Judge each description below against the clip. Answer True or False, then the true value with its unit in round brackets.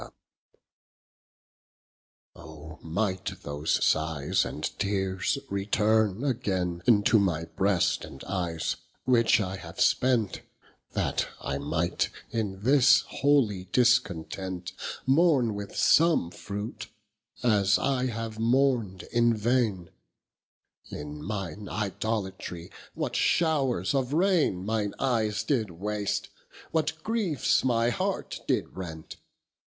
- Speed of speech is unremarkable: False (105 wpm)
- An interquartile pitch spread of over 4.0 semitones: True (5.1 semitones)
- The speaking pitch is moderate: False (105 Hz)